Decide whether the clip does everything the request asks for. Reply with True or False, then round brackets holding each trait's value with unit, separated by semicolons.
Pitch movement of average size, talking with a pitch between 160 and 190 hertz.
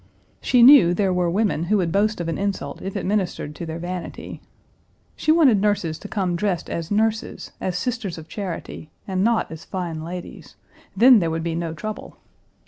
True (3.9 semitones; 185 Hz)